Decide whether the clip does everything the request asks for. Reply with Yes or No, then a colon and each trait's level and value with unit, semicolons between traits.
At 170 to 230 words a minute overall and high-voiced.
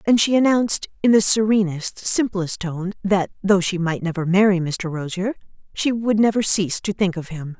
Yes: average, 190 wpm; high, 195 Hz